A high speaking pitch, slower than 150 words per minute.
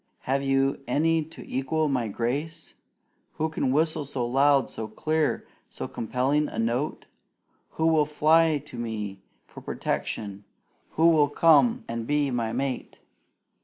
No: medium, 140 Hz; average, 140 wpm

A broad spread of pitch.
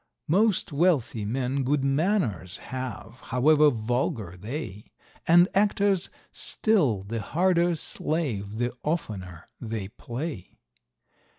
Yes: wide, 7.4 semitones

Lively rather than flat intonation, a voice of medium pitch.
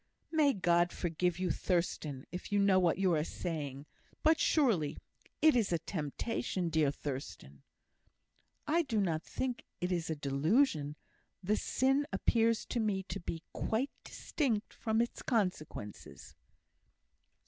Yes: wide, 6.5 semitones; medium, 180 Hz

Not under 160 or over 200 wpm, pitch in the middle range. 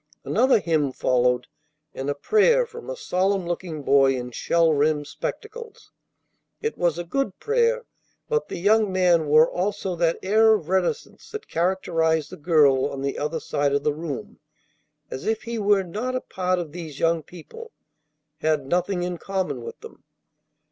Yes: average, 170 wpm; medium, 175 Hz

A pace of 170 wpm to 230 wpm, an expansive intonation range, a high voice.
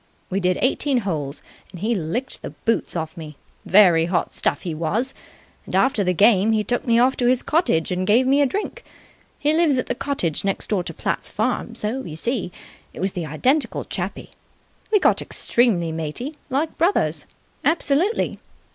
Yes: average, 180 wpm; wide, 7.2 semitones; high, 220 Hz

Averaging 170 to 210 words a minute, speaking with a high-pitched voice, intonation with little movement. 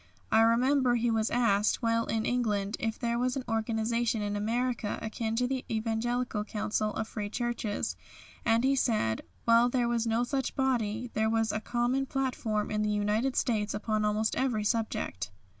Yes: average, 175 wpm; high, 225 Hz; narrow, 2.2 semitones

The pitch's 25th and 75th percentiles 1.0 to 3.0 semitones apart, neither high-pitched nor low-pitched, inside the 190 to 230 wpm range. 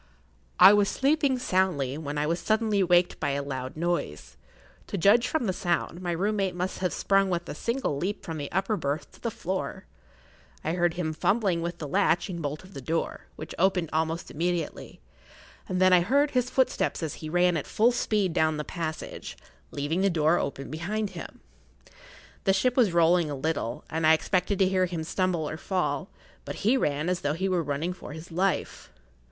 No: average, 3.6 semitones; medium, 175 Hz; fast, 205 wpm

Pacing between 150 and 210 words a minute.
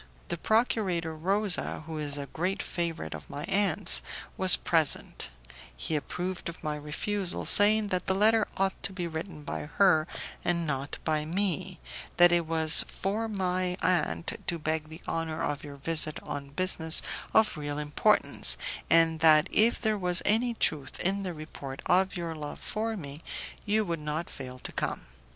Yes: average, 170 wpm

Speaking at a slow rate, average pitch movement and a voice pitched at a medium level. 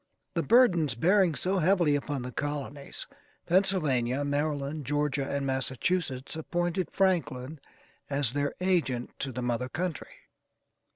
Yes: slow, 120 wpm; average, 4.7 semitones; medium, 145 Hz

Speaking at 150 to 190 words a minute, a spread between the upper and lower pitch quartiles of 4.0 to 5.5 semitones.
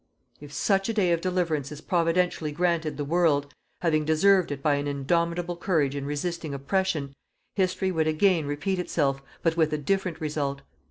No: average, 170 wpm; average, 3.6 semitones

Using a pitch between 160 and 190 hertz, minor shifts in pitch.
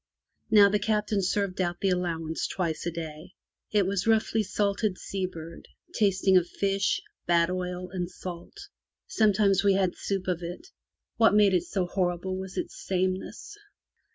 Yes: medium, 185 Hz; narrow, 2.2 semitones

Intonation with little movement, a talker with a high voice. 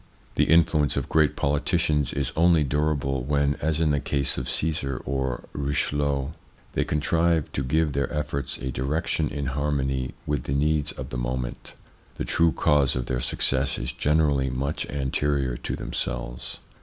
No: narrow, 2.2 semitones; very low, 70 Hz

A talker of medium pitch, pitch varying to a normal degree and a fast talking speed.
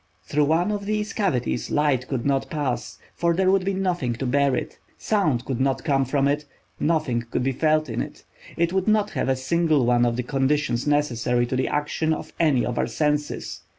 Yes: medium, 145 Hz; average, 4.7 semitones; fast, 210 wpm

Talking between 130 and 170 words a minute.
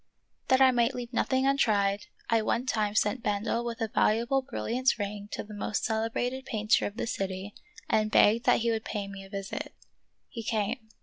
No: average, 185 wpm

